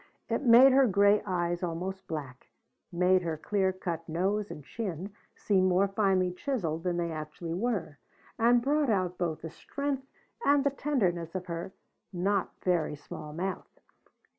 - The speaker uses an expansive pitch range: No, average, 3.9 semitones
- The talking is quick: No, average, 155 wpm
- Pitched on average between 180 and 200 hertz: Yes, medium, 185 Hz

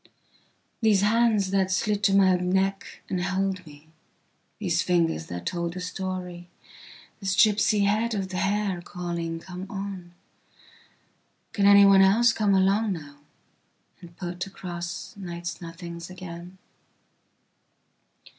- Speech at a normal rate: No, slow, 105 wpm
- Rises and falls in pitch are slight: Yes, narrow, 2.3 semitones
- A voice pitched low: No, medium, 185 Hz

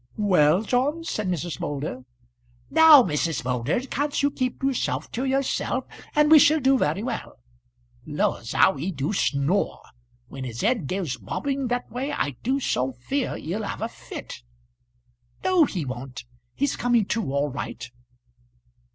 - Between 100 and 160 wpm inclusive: Yes, average, 150 wpm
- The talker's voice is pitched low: No, high, 205 Hz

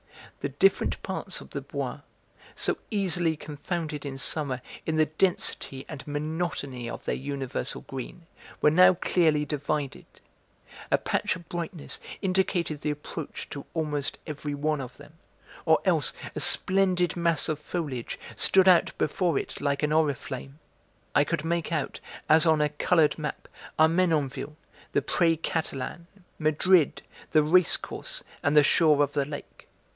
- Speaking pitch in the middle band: Yes, medium, 155 Hz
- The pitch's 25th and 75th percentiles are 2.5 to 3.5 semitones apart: Yes, average, 2.8 semitones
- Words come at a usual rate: Yes, average, 150 wpm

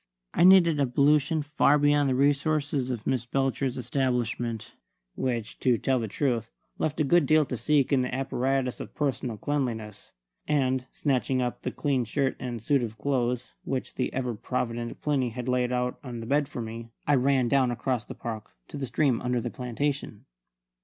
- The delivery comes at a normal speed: Yes, average, 180 wpm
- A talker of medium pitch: No, low, 130 Hz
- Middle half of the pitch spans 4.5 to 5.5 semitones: No, average, 2.8 semitones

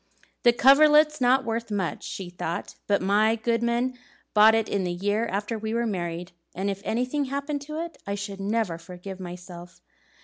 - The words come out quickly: No, average, 170 wpm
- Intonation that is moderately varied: Yes, average, 4.5 semitones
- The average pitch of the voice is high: Yes, high, 215 Hz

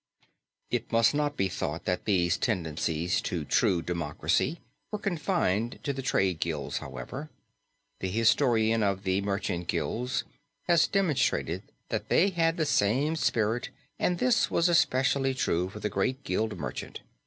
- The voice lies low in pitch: Yes, low, 110 Hz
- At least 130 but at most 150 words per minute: Yes, average, 145 wpm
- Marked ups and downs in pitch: Yes, wide, 8.1 semitones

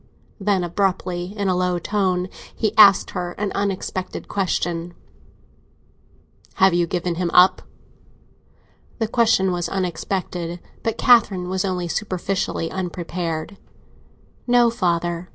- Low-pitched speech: No, medium, 185 Hz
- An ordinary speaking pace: No, slow, 115 wpm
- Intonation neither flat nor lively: No, narrow, 2.2 semitones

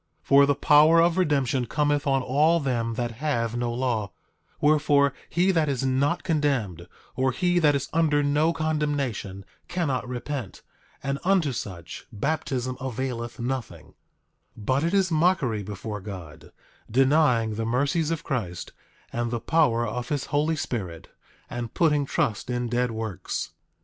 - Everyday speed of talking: Yes, average, 150 wpm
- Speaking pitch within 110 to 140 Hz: Yes, low, 135 Hz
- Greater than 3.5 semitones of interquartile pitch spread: Yes, average, 4.4 semitones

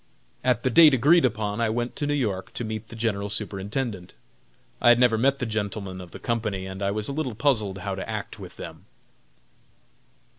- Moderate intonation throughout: Yes, average, 3.8 semitones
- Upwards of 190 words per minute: Yes, average, 200 wpm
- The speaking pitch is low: Yes, low, 110 Hz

